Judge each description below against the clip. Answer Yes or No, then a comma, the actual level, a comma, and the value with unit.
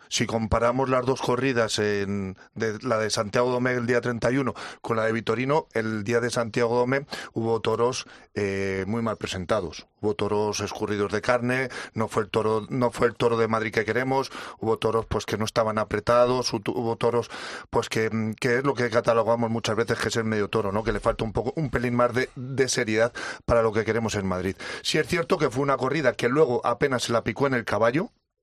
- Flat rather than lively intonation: Yes, narrow, 2.1 semitones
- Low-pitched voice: Yes, low, 115 Hz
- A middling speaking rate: No, fast, 215 wpm